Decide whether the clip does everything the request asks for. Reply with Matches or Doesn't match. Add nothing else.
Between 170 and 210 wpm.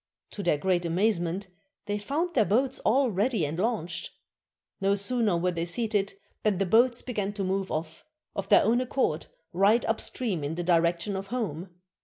Matches